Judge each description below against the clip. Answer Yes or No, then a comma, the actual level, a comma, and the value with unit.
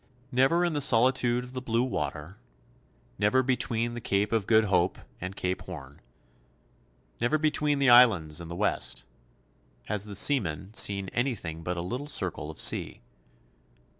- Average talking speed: Yes, average, 155 wpm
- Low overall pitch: Yes, low, 110 Hz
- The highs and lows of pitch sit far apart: Yes, wide, 5.8 semitones